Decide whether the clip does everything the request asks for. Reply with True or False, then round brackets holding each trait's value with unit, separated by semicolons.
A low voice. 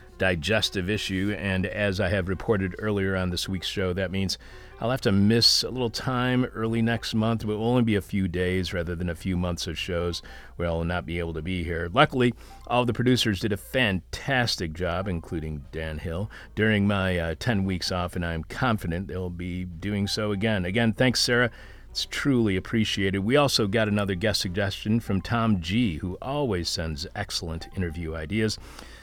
True (95 Hz)